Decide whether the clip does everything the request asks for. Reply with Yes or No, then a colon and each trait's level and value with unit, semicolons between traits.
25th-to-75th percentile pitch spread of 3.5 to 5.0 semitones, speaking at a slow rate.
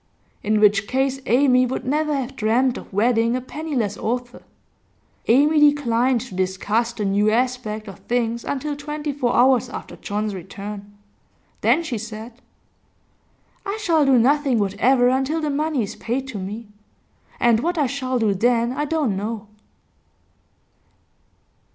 No: average, 4.2 semitones; average, 145 wpm